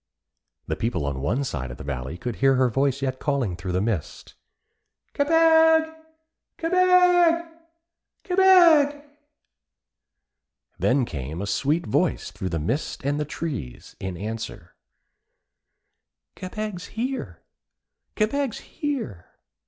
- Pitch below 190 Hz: Yes, medium, 140 Hz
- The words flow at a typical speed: No, slow, 115 wpm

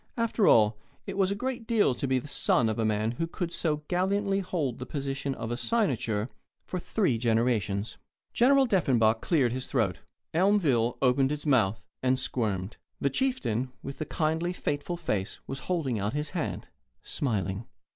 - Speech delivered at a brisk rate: No, average, 170 wpm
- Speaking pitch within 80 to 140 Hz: Yes, low, 135 Hz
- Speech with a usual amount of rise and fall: No, wide, 7.6 semitones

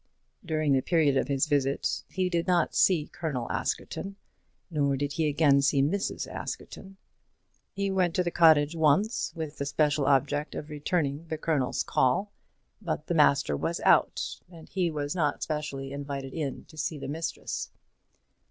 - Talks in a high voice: No, medium, 150 Hz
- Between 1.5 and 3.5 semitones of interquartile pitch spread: Yes, average, 3.1 semitones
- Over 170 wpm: No, average, 160 wpm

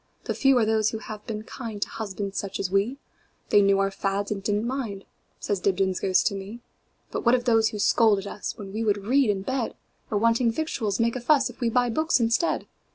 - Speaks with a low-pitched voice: No, high, 215 Hz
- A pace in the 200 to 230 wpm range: Yes, fast, 205 wpm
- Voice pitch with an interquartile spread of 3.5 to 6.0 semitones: No, average, 3.0 semitones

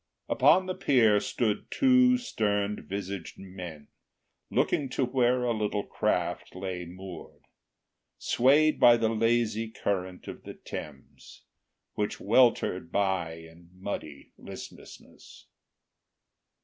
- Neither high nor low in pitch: No, low, 105 Hz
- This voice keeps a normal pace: No, slow, 110 wpm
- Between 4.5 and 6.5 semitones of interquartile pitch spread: Yes, average, 4.8 semitones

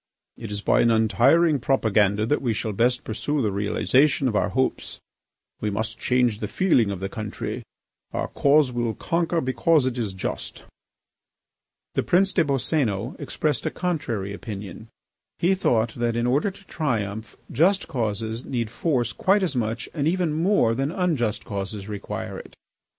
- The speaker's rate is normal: Yes, average, 160 wpm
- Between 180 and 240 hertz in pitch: No, low, 120 Hz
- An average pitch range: No, wide, 5.7 semitones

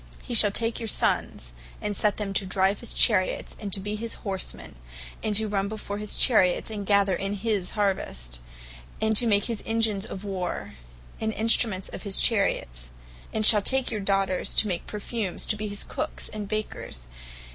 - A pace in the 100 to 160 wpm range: No, average, 185 wpm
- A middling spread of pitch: No, narrow, 2.0 semitones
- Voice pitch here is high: Yes, high, 205 Hz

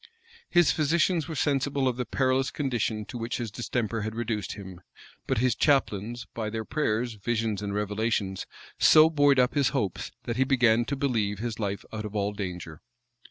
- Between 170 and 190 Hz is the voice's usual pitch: No, low, 115 Hz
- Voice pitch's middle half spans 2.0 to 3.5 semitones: No, average, 4.1 semitones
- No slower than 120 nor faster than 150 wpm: No, average, 180 wpm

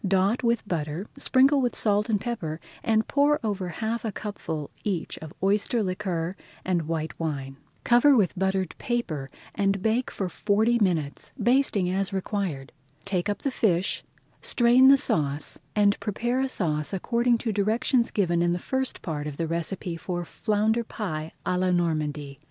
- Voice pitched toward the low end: No, high, 195 Hz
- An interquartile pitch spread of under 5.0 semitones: No, wide, 5.5 semitones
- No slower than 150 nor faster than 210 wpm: Yes, average, 165 wpm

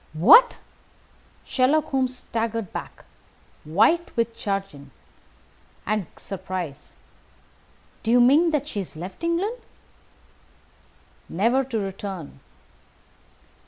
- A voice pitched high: Yes, high, 225 Hz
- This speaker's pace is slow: Yes, slow, 90 wpm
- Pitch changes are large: Yes, wide, 6.3 semitones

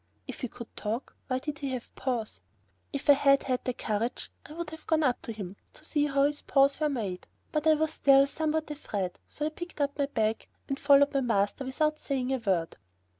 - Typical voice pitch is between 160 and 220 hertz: No, very high, 275 Hz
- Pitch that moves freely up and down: No, average, 4.0 semitones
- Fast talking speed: Yes, fast, 225 wpm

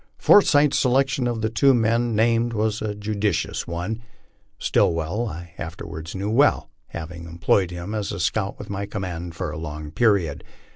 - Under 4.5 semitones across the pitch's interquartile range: No, average, 5.3 semitones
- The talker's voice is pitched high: No, low, 100 Hz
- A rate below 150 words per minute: No, average, 155 wpm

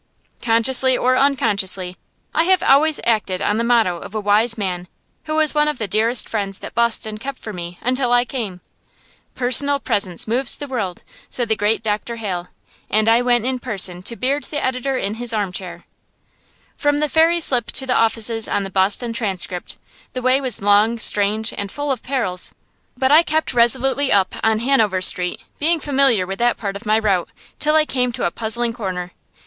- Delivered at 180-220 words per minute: Yes, average, 190 wpm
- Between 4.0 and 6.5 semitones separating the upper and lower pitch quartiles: Yes, average, 4.5 semitones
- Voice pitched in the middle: No, high, 230 Hz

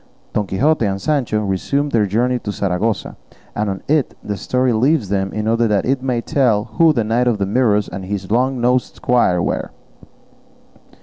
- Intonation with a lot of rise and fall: No, average, 3.9 semitones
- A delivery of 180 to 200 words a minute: Yes, average, 185 wpm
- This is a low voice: Yes, low, 115 Hz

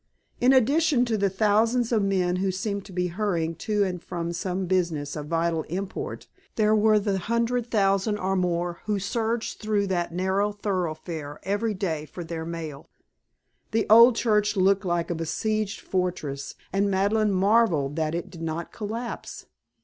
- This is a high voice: Yes, high, 195 Hz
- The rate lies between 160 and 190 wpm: Yes, average, 165 wpm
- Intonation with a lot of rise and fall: No, average, 3.9 semitones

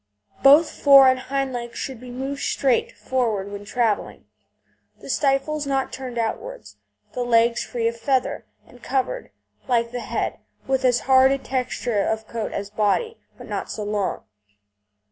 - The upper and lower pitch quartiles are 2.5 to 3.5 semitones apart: Yes, average, 2.8 semitones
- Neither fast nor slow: Yes, average, 160 wpm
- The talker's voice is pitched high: Yes, very high, 255 Hz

